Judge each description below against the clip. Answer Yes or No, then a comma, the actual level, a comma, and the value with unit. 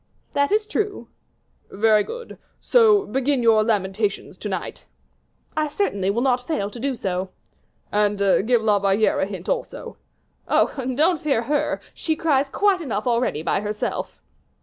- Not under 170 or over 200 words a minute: No, average, 150 wpm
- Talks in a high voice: Yes, high, 235 Hz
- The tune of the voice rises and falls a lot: Yes, wide, 6.8 semitones